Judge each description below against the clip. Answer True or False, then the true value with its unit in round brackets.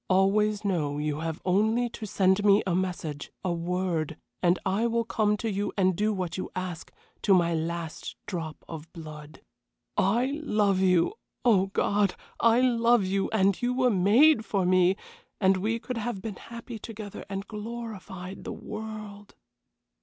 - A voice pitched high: True (195 Hz)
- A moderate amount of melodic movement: True (3.3 semitones)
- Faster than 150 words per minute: True (160 wpm)